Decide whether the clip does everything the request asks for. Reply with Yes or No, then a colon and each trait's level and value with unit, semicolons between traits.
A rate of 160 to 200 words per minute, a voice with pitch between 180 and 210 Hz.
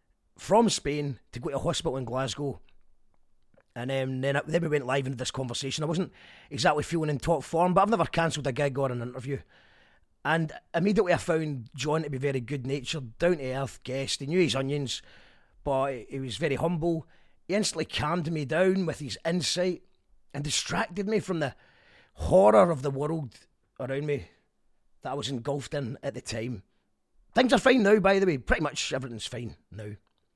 No: average, 190 wpm; medium, 145 Hz